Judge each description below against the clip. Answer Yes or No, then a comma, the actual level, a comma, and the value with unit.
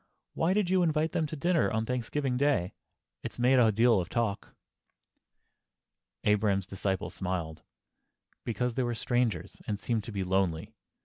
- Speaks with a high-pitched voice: No, low, 115 Hz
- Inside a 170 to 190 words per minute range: No, average, 150 wpm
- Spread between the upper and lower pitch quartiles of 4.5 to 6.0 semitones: Yes, average, 5.3 semitones